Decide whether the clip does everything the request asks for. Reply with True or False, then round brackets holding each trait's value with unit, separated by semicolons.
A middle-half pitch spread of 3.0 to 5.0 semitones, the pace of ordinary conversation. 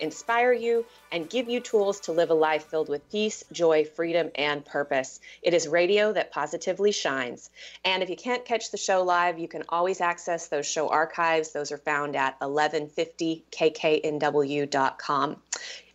True (3.9 semitones; 160 wpm)